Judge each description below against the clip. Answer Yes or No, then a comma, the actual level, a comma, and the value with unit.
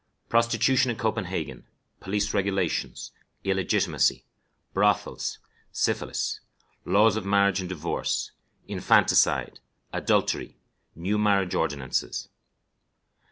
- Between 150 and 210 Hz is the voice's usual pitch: No, low, 100 Hz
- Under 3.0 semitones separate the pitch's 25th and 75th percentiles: Yes, narrow, 2.6 semitones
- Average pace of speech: No, slow, 80 wpm